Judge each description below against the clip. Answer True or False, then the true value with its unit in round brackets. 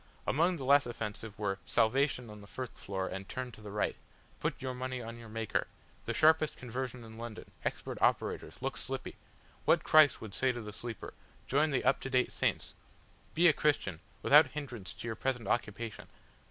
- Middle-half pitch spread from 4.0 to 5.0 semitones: False (3.6 semitones)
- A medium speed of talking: True (190 wpm)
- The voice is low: True (120 Hz)